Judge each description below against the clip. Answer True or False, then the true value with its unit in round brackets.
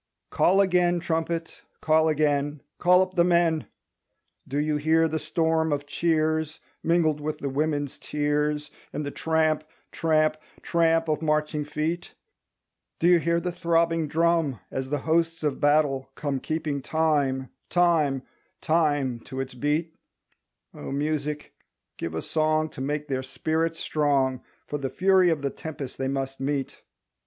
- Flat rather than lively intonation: True (2.3 semitones)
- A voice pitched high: False (155 Hz)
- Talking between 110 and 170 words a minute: True (145 wpm)